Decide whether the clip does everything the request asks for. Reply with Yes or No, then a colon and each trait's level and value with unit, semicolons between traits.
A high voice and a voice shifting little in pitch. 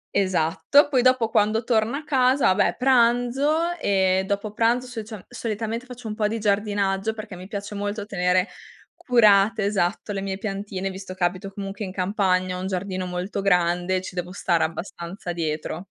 No: high, 200 Hz; average, 3.5 semitones